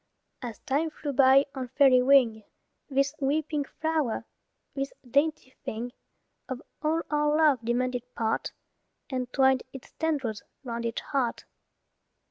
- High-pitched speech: Yes, very high, 270 Hz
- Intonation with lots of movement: No, average, 3.1 semitones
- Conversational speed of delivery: No, slow, 130 wpm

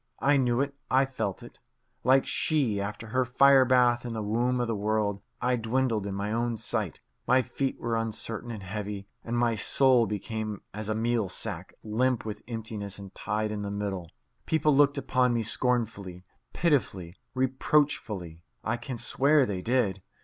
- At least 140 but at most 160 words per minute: No, average, 170 wpm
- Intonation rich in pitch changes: No, average, 3.7 semitones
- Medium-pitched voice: No, low, 115 Hz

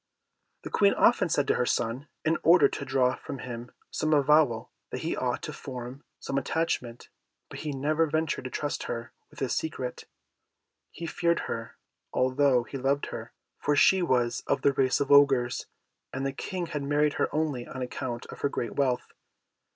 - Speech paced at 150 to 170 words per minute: No, average, 180 wpm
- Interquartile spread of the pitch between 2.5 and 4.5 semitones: Yes, average, 3.2 semitones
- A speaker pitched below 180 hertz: Yes, medium, 140 Hz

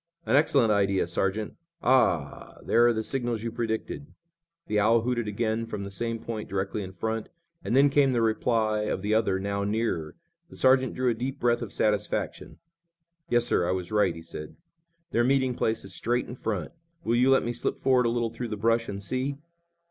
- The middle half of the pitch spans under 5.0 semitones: Yes, average, 3.0 semitones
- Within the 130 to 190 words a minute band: No, average, 200 wpm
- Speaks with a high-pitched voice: No, low, 115 Hz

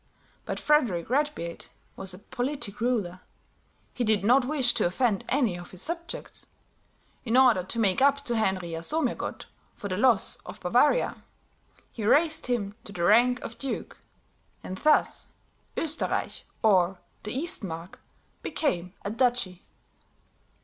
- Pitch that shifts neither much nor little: No, wide, 6.0 semitones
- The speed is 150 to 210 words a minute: No, slow, 135 wpm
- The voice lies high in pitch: Yes, high, 230 Hz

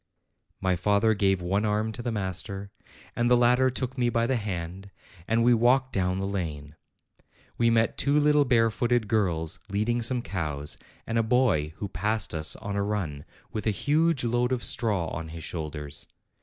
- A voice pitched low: Yes, low, 105 Hz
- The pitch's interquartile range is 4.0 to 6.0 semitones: Yes, average, 4.6 semitones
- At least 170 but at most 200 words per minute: Yes, average, 180 wpm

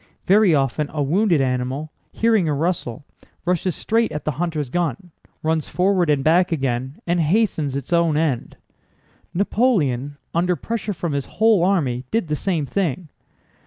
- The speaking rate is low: No, average, 155 wpm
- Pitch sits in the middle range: Yes, medium, 160 Hz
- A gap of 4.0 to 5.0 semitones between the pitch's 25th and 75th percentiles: Yes, average, 4.5 semitones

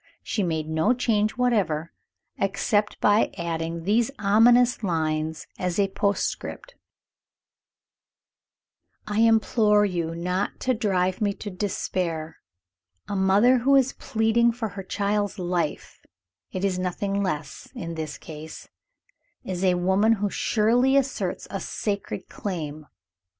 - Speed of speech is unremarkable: No, slow, 125 wpm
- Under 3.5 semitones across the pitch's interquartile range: No, average, 4.3 semitones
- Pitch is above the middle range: Yes, high, 200 Hz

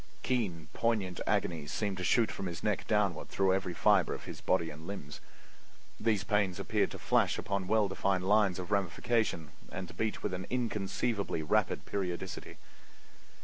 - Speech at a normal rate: Yes, average, 165 wpm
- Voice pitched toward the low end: Yes, very low, 95 Hz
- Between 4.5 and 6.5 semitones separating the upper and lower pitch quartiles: No, average, 2.7 semitones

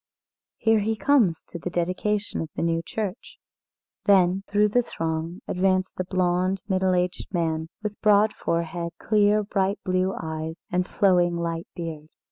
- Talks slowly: No, average, 155 wpm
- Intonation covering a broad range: No, average, 3.3 semitones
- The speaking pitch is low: No, medium, 185 Hz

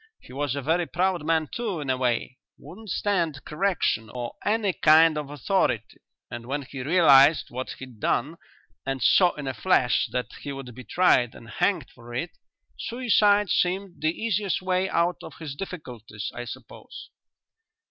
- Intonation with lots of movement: Yes, wide, 6.1 semitones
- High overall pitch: No, medium, 155 Hz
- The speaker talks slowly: No, average, 170 wpm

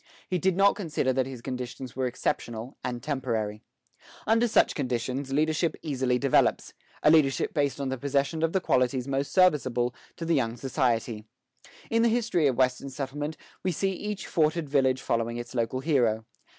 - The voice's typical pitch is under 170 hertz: Yes, low, 135 Hz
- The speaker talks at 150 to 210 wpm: Yes, average, 170 wpm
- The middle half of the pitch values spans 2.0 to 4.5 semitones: Yes, average, 4.2 semitones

